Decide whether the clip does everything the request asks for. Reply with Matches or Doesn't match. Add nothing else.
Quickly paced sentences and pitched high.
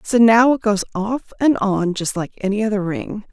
Matches